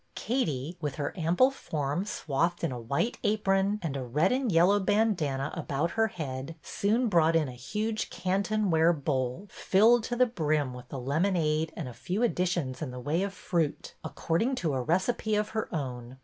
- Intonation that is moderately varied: No, wide, 6.5 semitones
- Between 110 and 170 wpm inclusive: No, average, 185 wpm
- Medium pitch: Yes, medium, 170 Hz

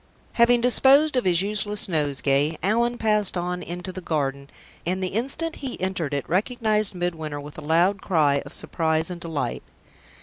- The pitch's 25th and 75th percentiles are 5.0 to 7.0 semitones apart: Yes, wide, 5.4 semitones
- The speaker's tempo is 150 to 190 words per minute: Yes, average, 165 wpm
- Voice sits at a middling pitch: Yes, medium, 180 Hz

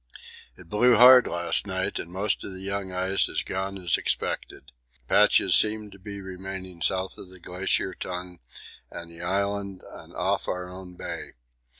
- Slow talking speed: No, average, 170 wpm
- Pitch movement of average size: No, narrow, 1.6 semitones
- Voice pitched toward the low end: Yes, very low, 95 Hz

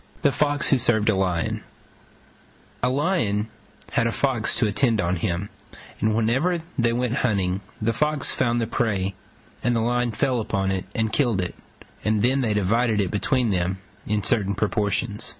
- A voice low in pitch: Yes, low, 110 Hz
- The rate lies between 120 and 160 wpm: No, average, 170 wpm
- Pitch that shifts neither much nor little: Yes, average, 3.6 semitones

